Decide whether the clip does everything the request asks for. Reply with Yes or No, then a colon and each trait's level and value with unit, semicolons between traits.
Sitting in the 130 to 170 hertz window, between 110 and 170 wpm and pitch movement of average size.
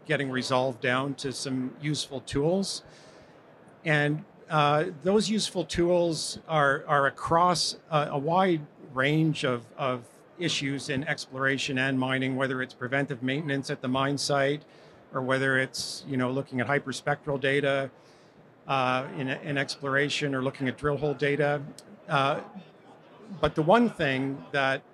No: medium, 140 Hz; average, 140 wpm; narrow, 2.2 semitones